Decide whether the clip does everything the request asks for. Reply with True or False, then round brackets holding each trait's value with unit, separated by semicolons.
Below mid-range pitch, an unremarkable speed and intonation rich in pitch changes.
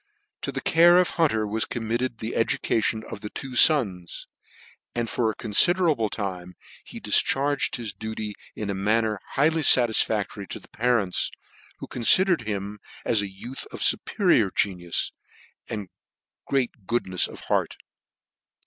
False (110 Hz; 150 wpm; 4.2 semitones)